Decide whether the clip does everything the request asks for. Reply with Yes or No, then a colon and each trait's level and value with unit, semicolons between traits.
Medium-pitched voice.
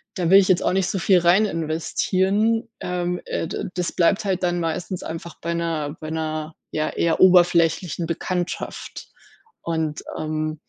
Yes: medium, 170 Hz